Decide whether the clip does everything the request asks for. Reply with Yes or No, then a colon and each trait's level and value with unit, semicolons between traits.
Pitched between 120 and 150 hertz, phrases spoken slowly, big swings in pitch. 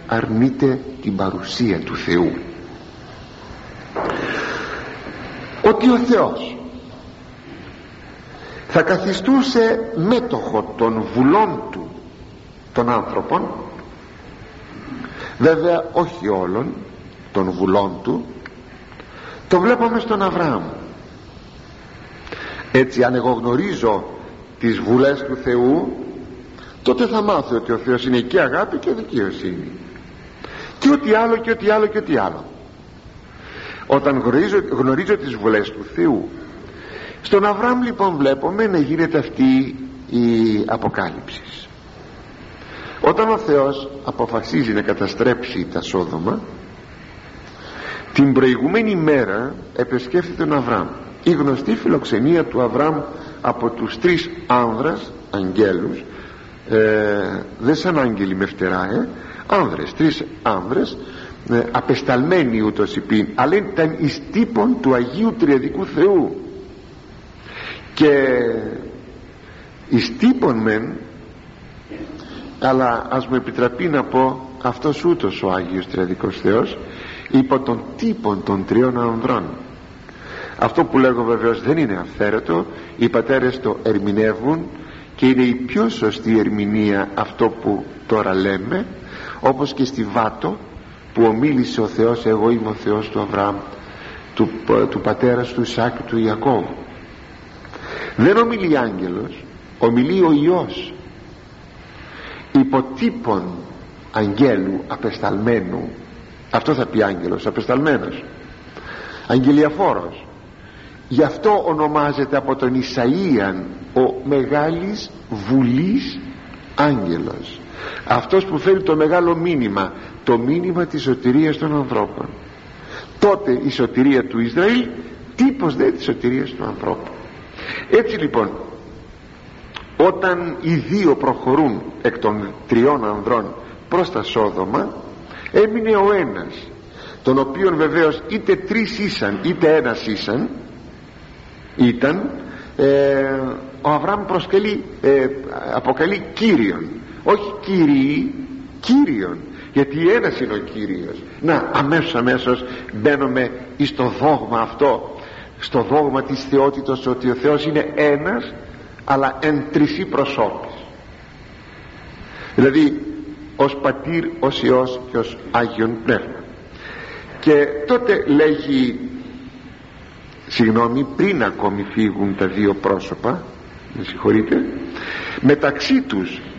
Yes: low, 135 Hz; slow, 105 wpm; wide, 7.2 semitones